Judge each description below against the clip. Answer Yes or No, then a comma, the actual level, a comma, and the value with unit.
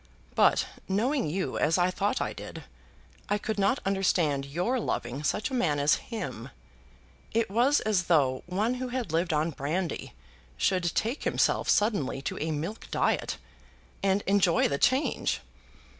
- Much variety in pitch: Yes, wide, 6.0 semitones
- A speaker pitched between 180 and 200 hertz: Yes, medium, 185 Hz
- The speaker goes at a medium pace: Yes, average, 155 wpm